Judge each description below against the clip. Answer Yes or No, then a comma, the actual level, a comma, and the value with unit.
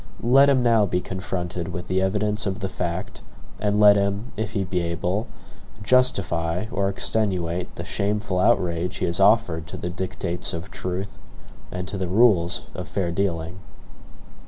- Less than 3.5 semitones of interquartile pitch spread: Yes, average, 2.9 semitones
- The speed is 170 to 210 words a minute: No, average, 160 wpm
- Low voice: Yes, very low, 95 Hz